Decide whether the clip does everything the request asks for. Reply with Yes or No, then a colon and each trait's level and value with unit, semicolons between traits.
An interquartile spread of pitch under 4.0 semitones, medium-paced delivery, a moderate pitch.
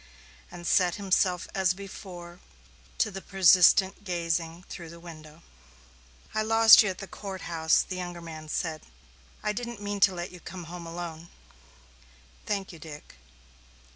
Yes: narrow, 2.6 semitones; average, 150 wpm; medium, 180 Hz